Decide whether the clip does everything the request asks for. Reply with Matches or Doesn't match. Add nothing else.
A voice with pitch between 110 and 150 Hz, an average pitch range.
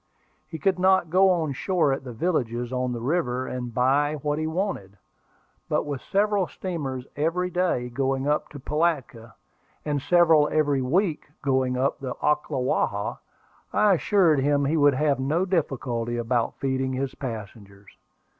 Matches